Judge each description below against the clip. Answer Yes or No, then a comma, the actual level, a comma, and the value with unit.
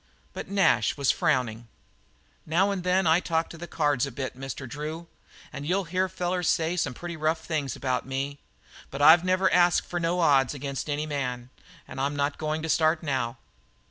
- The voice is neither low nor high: Yes, medium, 155 Hz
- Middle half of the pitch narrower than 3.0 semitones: No, average, 4.1 semitones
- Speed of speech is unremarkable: Yes, average, 185 wpm